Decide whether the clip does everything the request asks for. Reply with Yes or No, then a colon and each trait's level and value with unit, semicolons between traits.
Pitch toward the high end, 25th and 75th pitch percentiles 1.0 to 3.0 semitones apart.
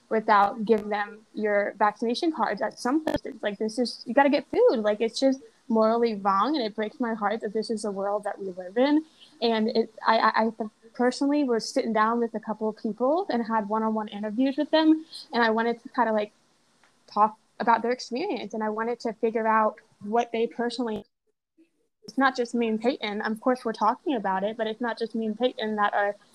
Yes: high, 225 Hz; narrow, 2.5 semitones